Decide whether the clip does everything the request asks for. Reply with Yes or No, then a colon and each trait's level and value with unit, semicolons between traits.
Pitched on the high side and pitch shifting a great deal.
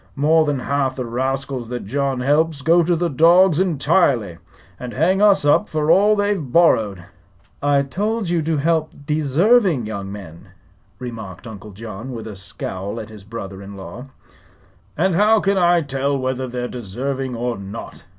No: low, 135 Hz; wide, 6.2 semitones